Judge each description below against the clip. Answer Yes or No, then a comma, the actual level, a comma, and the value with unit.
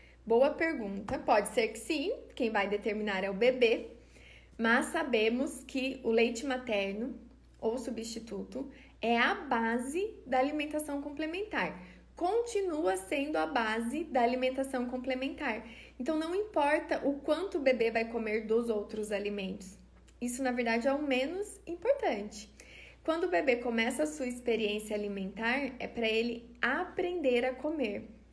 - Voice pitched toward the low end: No, very high, 255 Hz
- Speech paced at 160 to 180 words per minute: No, average, 140 wpm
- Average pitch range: Yes, average, 5.0 semitones